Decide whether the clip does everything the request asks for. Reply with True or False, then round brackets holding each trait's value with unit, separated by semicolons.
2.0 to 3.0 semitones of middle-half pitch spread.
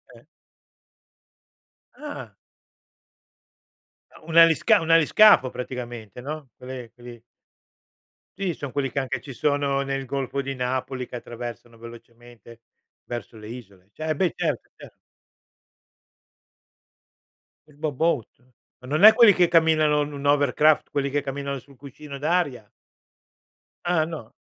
False (4.0 semitones)